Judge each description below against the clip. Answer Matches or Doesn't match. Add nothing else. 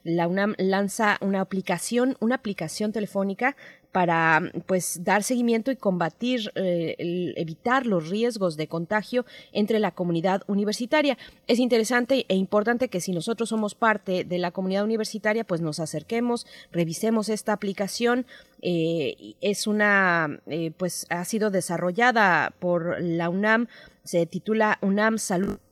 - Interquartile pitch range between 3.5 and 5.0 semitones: Matches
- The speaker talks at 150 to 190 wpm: Doesn't match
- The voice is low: Doesn't match